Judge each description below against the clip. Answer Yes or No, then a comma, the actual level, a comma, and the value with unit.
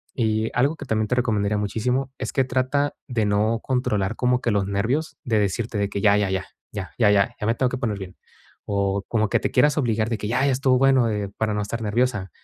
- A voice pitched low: Yes, low, 110 Hz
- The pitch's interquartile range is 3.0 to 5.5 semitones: Yes, average, 3.6 semitones